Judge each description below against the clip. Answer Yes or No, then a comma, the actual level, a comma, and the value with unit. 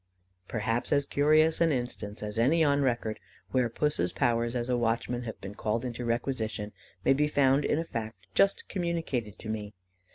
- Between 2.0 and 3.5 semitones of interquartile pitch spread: No, average, 4.3 semitones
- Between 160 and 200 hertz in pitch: No, low, 120 Hz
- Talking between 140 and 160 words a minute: No, average, 175 wpm